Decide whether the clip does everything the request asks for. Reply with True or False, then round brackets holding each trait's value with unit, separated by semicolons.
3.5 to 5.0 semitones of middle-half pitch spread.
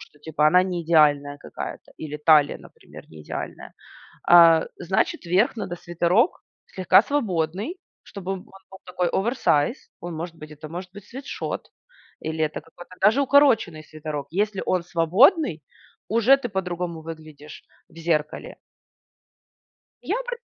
True (4.2 semitones)